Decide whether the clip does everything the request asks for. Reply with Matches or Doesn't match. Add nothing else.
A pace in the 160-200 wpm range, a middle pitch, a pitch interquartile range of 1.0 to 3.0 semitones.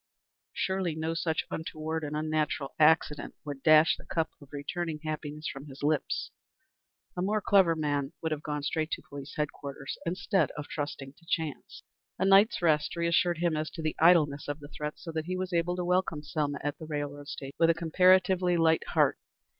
Matches